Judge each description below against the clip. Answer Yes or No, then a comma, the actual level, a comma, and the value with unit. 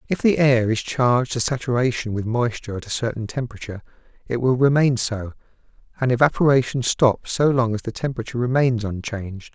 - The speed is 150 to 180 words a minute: Yes, average, 170 wpm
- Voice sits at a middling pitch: No, low, 120 Hz